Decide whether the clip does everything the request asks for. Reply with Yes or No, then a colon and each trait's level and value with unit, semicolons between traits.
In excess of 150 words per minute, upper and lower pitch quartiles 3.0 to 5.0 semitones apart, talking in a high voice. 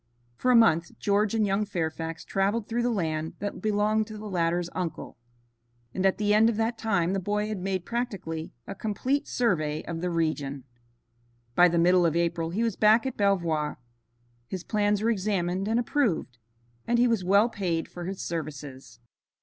Yes: average, 180 wpm; average, 4.3 semitones; high, 195 Hz